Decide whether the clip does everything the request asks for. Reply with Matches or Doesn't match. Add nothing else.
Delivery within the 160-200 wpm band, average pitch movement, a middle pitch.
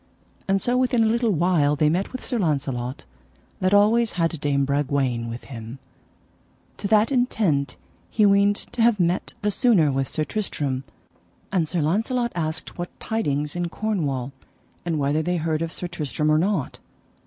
Doesn't match